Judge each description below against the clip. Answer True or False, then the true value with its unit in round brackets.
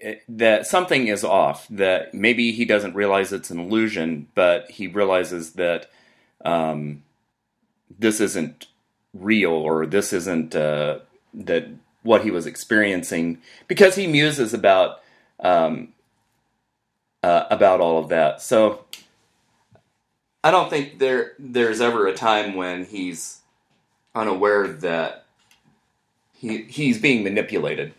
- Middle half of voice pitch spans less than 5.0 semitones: False (5.4 semitones)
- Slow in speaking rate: True (120 wpm)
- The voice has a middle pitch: False (105 Hz)